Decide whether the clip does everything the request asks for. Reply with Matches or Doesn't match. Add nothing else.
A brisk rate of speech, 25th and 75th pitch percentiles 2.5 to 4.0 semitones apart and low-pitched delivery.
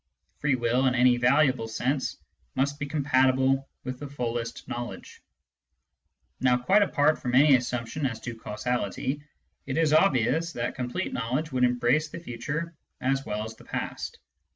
Doesn't match